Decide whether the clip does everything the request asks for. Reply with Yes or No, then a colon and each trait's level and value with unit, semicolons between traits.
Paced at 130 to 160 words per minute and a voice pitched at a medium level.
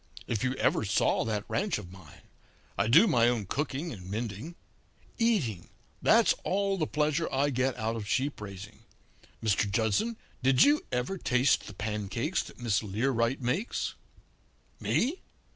No: average, 150 wpm; low, 120 Hz